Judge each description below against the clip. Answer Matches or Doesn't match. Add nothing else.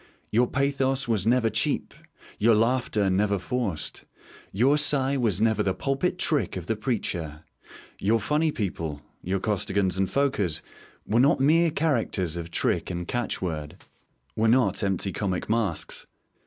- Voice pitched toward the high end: Doesn't match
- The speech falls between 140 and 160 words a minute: Matches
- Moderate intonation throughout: Doesn't match